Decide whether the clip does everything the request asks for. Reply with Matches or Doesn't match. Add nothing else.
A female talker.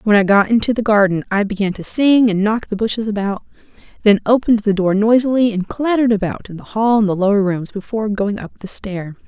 Matches